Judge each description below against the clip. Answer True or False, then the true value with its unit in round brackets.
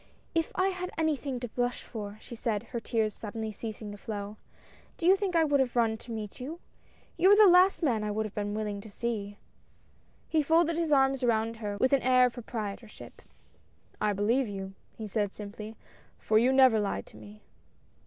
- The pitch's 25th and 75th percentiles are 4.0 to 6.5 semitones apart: True (4.5 semitones)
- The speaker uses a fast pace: True (210 wpm)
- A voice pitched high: True (230 Hz)